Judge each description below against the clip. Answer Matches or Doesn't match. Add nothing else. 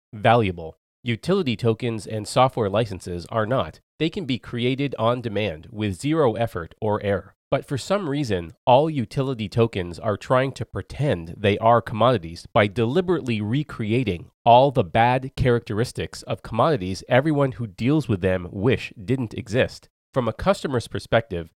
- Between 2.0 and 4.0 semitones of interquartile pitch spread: Doesn't match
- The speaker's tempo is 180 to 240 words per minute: Doesn't match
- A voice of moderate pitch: Doesn't match